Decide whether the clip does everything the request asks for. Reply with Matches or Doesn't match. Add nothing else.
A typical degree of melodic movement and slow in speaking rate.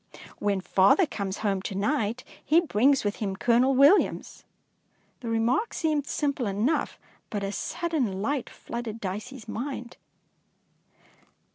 Doesn't match